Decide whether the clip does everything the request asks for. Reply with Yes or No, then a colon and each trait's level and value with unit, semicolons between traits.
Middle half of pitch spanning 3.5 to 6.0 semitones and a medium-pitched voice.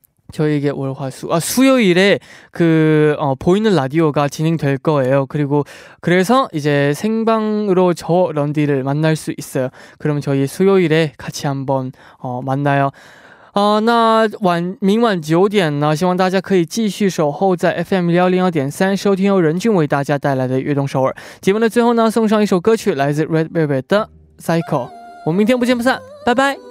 Yes: wide, 5.5 semitones; medium, 165 Hz